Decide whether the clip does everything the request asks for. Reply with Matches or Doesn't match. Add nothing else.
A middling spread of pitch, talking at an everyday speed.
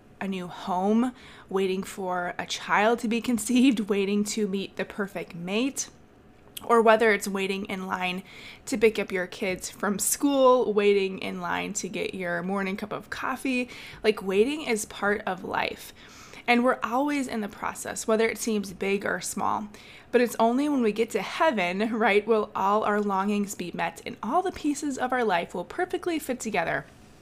Matches